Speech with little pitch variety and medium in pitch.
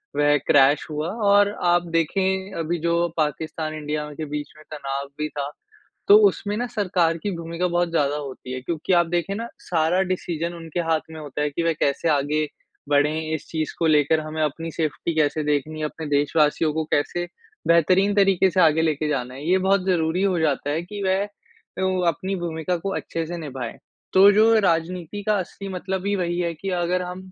No: average, 3.3 semitones; medium, 165 Hz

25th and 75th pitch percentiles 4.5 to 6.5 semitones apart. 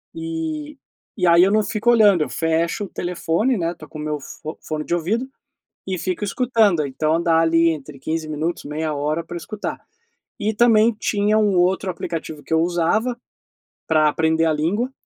Yes: average, 5.0 semitones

